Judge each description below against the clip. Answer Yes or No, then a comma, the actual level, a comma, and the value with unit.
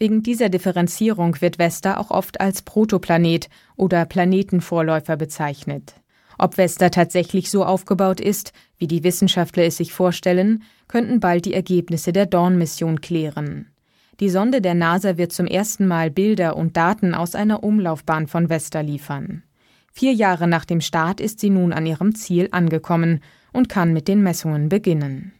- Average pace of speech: Yes, average, 155 wpm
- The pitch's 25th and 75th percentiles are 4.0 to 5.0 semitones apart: No, average, 2.7 semitones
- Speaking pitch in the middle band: Yes, medium, 180 Hz